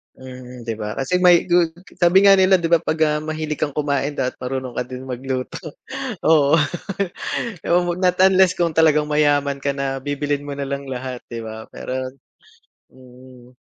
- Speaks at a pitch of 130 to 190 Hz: Yes, medium, 140 Hz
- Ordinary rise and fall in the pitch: Yes, average, 3.9 semitones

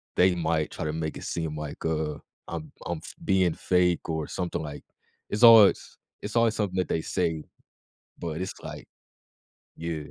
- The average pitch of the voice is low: Yes, very low, 85 Hz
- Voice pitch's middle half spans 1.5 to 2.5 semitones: No, average, 2.9 semitones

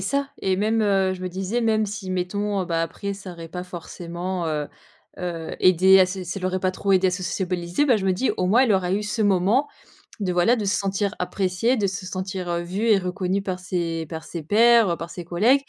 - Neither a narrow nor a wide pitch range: No, narrow, 2.3 semitones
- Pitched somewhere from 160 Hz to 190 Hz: Yes, medium, 185 Hz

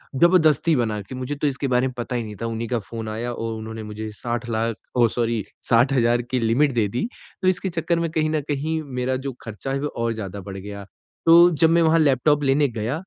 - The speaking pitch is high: No, low, 125 Hz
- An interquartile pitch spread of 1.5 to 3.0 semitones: No, average, 4.8 semitones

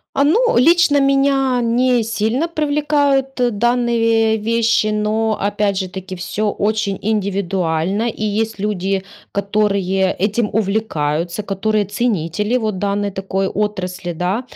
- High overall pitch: Yes, high, 210 Hz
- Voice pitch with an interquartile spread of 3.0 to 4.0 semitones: Yes, average, 3.4 semitones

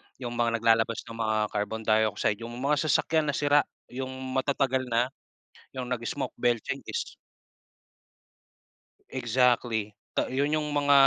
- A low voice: Yes, low, 125 Hz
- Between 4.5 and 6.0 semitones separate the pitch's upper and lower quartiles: No, average, 3.5 semitones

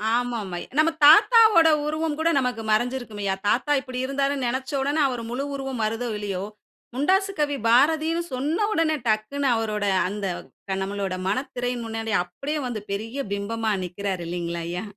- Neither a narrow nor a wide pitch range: No, wide, 5.7 semitones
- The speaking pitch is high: Yes, high, 245 Hz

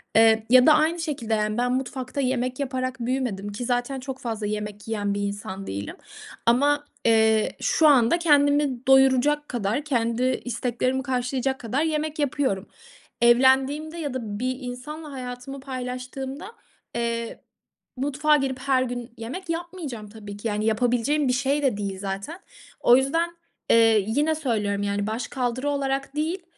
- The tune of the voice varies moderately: Yes, average, 3.9 semitones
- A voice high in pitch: Yes, very high, 255 Hz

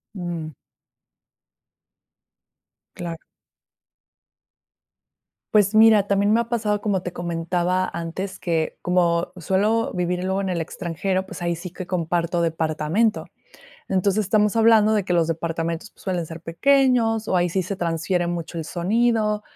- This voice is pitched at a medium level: Yes, medium, 180 Hz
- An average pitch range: Yes, average, 3.7 semitones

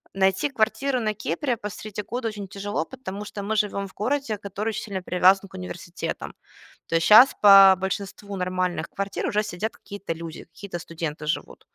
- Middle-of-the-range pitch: No, high, 200 Hz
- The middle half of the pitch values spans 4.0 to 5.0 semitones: No, average, 2.7 semitones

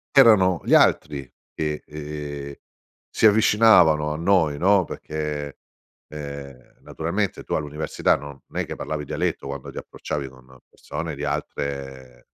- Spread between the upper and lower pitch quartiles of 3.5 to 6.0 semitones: No, average, 2.7 semitones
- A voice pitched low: Yes, very low, 75 Hz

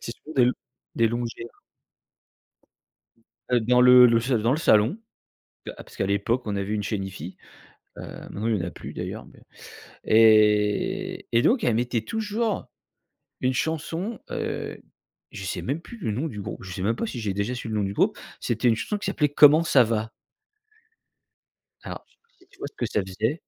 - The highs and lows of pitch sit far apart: Yes, wide, 5.8 semitones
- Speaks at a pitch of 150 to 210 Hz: No, low, 115 Hz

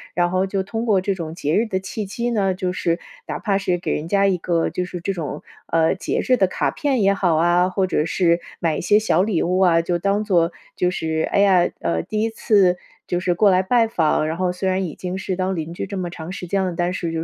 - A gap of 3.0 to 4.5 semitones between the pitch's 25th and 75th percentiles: No, narrow, 2.5 semitones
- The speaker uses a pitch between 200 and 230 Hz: No, medium, 185 Hz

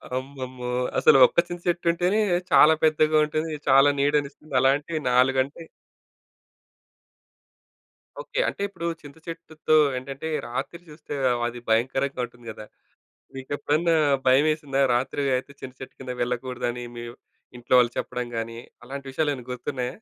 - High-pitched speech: No, low, 135 Hz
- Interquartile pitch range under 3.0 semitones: No, average, 3.5 semitones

